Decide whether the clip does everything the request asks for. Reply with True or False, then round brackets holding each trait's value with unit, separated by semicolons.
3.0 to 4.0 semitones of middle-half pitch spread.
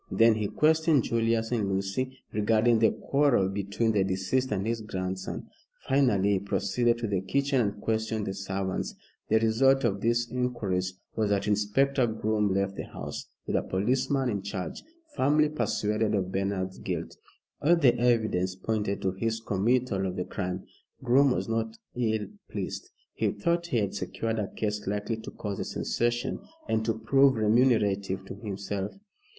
True (3.4 semitones)